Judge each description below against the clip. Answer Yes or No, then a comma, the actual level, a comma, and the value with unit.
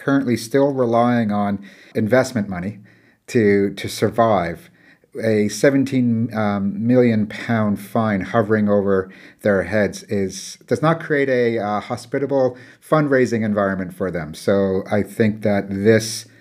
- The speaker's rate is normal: No, slow, 130 wpm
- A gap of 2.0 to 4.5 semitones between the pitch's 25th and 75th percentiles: Yes, average, 3.5 semitones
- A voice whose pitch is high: No, low, 110 Hz